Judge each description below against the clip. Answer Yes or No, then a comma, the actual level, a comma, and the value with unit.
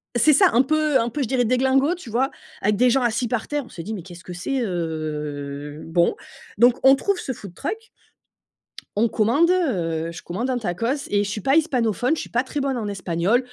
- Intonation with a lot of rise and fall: Yes, wide, 7.0 semitones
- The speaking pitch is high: Yes, high, 235 Hz